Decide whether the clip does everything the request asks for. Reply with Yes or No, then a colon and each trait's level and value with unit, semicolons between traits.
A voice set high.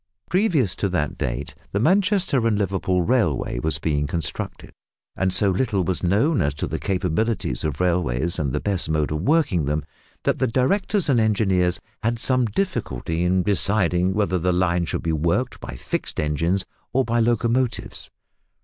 No: very low, 95 Hz